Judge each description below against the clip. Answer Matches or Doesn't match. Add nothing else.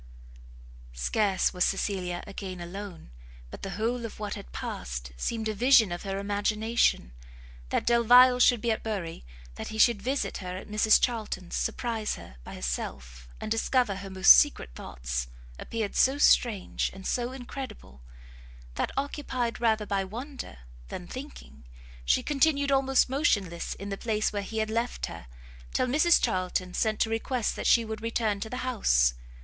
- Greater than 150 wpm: Matches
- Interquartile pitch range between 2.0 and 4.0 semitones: Doesn't match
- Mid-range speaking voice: Doesn't match